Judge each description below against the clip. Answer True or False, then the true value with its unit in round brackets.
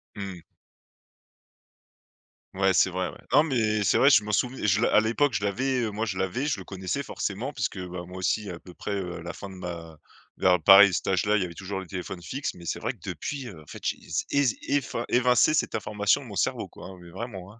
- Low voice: True (100 Hz)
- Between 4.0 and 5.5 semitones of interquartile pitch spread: True (4.4 semitones)